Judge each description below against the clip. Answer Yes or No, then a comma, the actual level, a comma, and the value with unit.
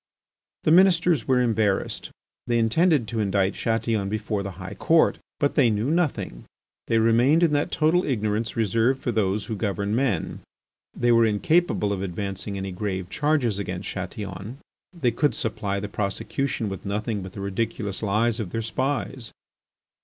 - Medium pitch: No, low, 110 Hz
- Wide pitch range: No, average, 4.6 semitones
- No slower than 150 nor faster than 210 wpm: Yes, average, 160 wpm